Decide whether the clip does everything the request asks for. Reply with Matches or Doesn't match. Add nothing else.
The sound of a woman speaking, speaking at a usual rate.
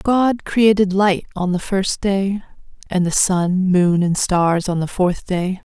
Matches